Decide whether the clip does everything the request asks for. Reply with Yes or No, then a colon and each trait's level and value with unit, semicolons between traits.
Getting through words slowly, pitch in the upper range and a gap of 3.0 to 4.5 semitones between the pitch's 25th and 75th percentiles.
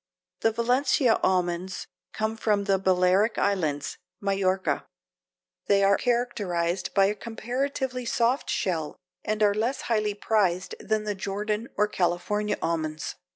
Yes: slow, 130 wpm; high, 205 Hz; average, 3.3 semitones